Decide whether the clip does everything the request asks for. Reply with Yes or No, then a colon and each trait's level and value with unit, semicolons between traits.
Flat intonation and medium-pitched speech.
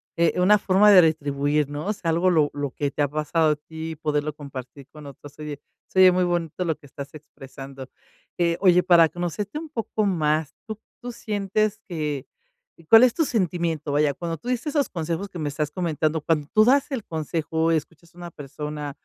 No: average, 3.8 semitones; medium, 160 Hz